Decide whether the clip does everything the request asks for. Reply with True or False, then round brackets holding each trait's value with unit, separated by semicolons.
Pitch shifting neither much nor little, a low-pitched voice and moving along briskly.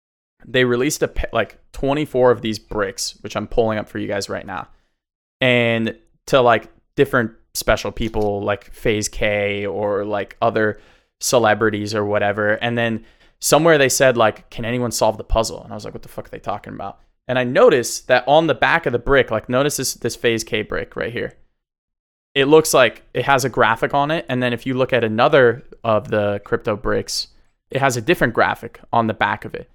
True (3.4 semitones; 115 Hz; 210 wpm)